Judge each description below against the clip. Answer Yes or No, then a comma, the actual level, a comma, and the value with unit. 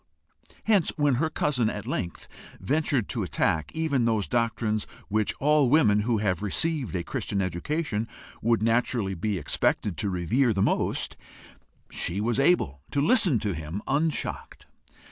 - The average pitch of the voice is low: Yes, low, 115 Hz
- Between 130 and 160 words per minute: Yes, average, 145 wpm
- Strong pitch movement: Yes, wide, 6.2 semitones